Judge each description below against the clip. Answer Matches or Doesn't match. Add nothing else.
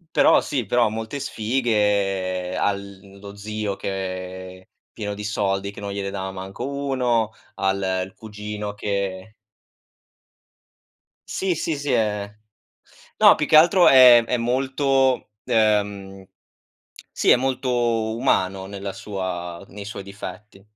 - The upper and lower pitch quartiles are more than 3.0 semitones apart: Matches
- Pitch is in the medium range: Doesn't match